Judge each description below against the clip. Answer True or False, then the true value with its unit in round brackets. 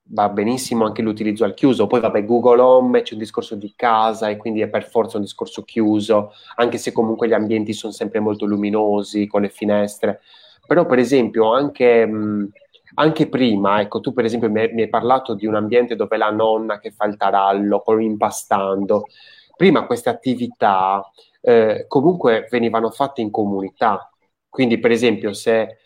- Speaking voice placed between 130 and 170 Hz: False (110 Hz)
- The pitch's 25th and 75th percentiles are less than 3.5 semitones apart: True (2.6 semitones)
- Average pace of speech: False (175 wpm)